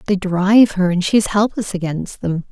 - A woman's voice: Yes, female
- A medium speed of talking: No, fast, 215 wpm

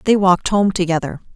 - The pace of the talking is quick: No, average, 175 wpm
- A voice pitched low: No, medium, 185 Hz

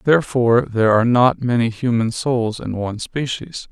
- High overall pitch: No, low, 120 Hz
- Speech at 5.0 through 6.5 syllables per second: Yes, 5.2 syllables/s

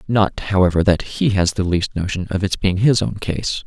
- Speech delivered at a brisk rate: Yes, fast, 230 wpm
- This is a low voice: Yes, low, 100 Hz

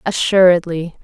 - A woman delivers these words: Yes, female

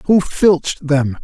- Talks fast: No, average, 145 wpm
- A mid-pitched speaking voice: Yes, medium, 160 Hz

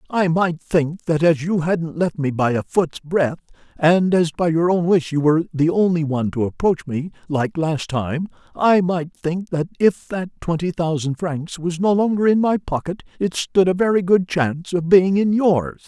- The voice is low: No, medium, 170 Hz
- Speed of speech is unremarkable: No, fast, 210 wpm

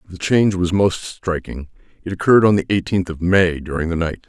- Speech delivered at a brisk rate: Yes, fast, 210 wpm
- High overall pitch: No, very low, 90 Hz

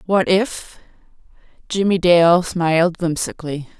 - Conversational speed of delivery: No, slow, 80 wpm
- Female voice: Yes, female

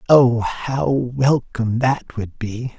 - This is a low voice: Yes, low, 125 Hz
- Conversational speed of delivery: No, slow, 130 wpm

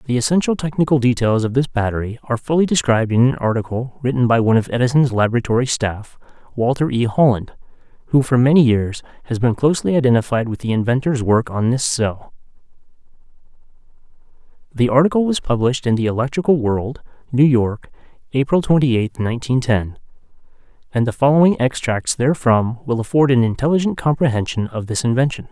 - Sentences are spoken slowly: No, average, 155 wpm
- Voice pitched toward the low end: Yes, low, 125 Hz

